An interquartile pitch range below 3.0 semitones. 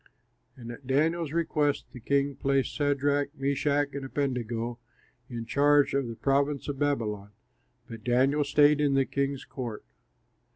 Yes: narrow, 2.5 semitones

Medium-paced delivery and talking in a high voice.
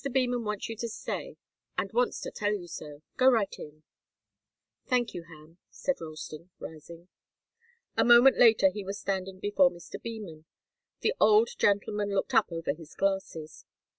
Yes: average, 160 wpm; high, 195 Hz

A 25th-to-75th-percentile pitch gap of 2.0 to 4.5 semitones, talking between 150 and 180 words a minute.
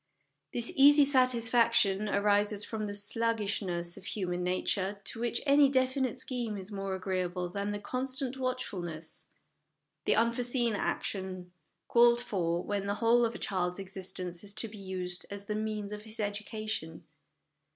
Yes: average, 3.7 semitones; average, 155 wpm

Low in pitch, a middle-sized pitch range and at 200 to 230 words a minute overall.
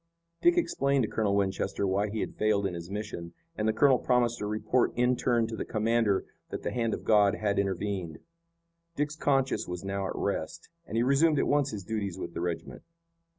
Yes: low, 110 Hz; average, 3.9 semitones; fast, 205 wpm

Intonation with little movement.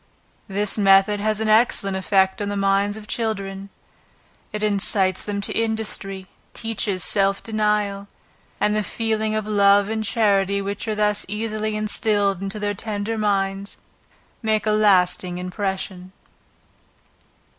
Yes: narrow, 1.5 semitones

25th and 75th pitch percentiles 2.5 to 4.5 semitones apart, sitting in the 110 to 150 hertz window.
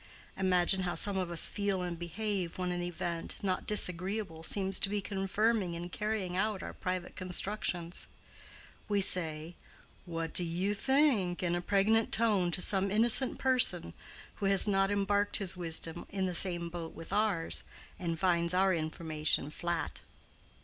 No: average, 2.9 semitones; medium, 185 Hz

